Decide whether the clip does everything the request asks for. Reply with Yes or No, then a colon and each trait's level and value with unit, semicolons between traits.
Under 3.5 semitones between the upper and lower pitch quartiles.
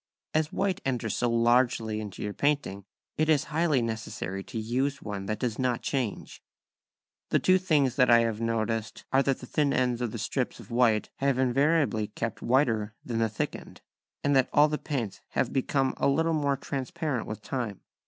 No: average, 4.1 semitones